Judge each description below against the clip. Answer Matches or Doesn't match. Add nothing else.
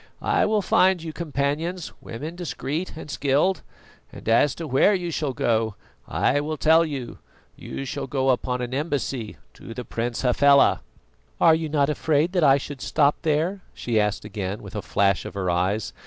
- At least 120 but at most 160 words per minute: Doesn't match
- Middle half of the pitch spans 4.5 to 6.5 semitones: Matches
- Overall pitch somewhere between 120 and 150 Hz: Matches